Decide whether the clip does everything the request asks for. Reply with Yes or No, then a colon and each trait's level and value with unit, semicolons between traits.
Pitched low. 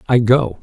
Yes: low, 115 Hz